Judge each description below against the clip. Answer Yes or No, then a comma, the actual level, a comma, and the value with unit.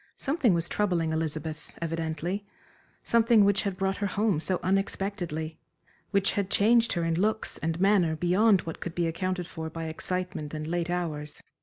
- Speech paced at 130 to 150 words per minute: No, average, 165 wpm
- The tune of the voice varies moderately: Yes, average, 3.6 semitones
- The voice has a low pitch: No, medium, 175 Hz